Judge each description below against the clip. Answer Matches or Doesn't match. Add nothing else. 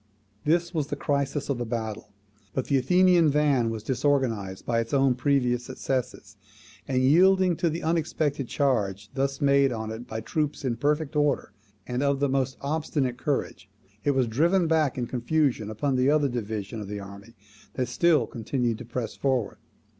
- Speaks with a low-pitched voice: Matches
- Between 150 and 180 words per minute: Matches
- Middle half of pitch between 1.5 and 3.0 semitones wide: Doesn't match